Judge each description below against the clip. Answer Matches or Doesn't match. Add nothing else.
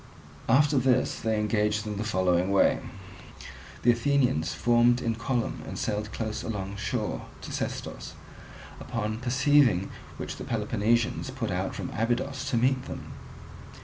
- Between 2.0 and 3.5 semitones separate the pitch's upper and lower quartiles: Matches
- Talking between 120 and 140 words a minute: Matches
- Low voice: Matches